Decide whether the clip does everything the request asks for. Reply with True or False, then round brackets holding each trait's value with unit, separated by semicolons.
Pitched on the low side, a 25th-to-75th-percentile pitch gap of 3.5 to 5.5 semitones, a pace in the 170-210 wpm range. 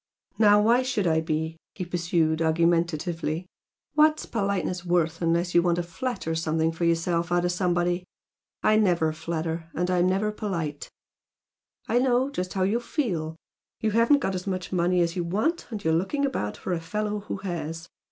False (175 Hz; 3.9 semitones; 175 wpm)